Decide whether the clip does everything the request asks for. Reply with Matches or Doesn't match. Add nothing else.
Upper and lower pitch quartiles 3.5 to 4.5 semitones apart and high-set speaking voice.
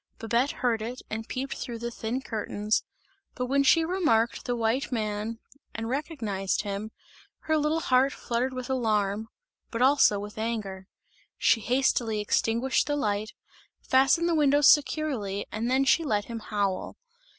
Matches